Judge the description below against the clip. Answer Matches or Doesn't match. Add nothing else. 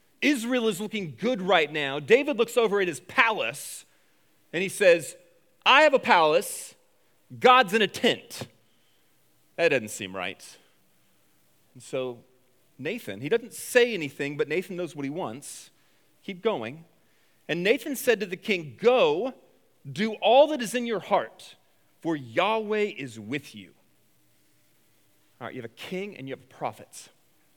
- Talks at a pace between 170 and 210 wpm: Doesn't match